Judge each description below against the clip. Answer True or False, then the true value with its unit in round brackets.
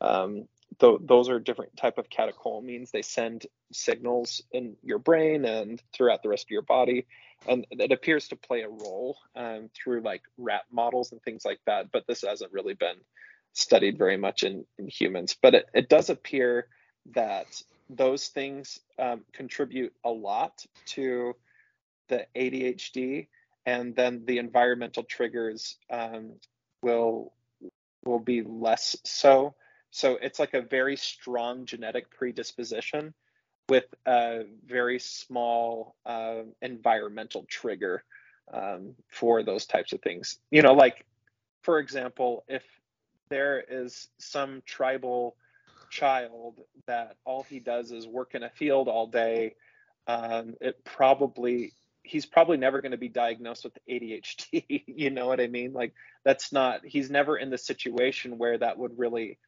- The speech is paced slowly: False (145 wpm)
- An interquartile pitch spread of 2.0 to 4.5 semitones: True (2.4 semitones)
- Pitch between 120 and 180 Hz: True (125 Hz)